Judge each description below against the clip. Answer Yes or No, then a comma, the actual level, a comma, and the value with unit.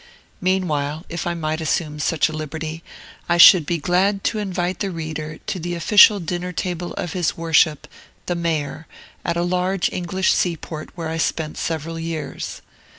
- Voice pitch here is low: No, medium, 170 Hz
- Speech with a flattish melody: Yes, narrow, 2.3 semitones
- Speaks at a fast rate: No, average, 165 wpm